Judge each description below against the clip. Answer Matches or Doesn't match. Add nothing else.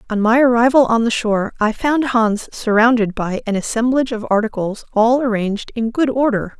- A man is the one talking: Doesn't match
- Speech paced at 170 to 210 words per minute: Matches